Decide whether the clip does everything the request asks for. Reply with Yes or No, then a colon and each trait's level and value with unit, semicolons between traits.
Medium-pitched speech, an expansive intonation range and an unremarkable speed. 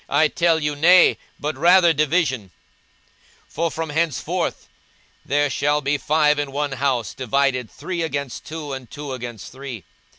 No: medium, 145 Hz; average, 3.0 semitones; average, 155 wpm